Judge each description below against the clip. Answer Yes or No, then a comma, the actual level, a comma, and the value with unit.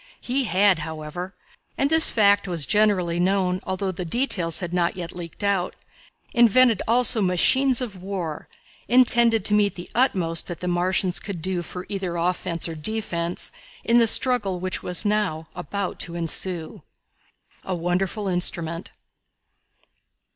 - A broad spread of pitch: No, average, 3.5 semitones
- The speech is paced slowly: No, average, 145 wpm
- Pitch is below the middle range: No, medium, 185 Hz